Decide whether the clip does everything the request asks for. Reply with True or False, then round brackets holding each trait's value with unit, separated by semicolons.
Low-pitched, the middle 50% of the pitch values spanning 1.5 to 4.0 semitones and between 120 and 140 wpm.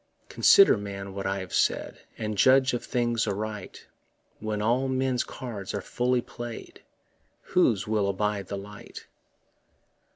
True (110 Hz; 3.5 semitones; 135 wpm)